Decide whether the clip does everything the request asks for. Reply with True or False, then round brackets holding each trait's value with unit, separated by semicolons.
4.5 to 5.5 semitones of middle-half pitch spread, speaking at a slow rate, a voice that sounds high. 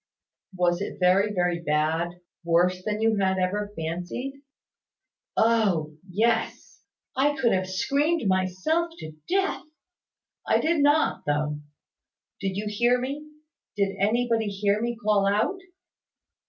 True (4.8 semitones; 125 wpm; 205 Hz)